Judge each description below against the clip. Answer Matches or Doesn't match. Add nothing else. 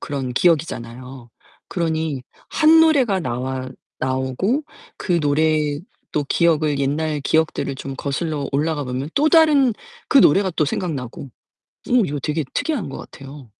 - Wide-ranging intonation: Doesn't match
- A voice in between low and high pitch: Matches